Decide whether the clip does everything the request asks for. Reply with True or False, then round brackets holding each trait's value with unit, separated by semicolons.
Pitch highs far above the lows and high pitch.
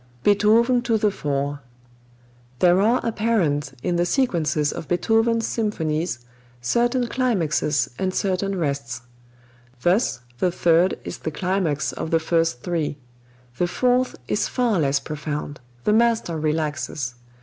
False (6.6 semitones; 175 Hz)